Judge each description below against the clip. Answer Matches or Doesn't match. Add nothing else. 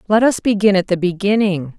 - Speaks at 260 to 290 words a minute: Doesn't match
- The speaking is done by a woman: Matches